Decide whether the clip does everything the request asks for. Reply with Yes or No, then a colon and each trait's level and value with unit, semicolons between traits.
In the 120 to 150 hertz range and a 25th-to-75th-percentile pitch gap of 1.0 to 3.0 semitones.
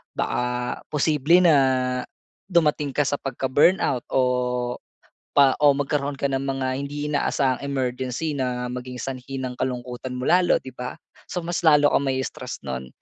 Yes: low, 135 Hz; narrow, 2.6 semitones